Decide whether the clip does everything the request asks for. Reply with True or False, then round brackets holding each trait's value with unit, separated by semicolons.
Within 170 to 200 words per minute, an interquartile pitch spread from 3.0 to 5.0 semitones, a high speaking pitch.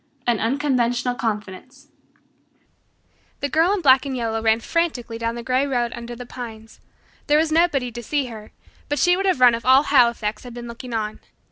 True (190 wpm; 3.4 semitones; 245 Hz)